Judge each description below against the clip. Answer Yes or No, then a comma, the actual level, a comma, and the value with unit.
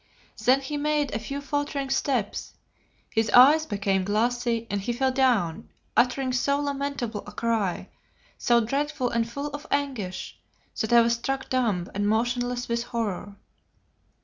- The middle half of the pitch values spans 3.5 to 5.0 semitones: Yes, average, 3.9 semitones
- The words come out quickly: No, average, 150 wpm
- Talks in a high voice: Yes, high, 245 Hz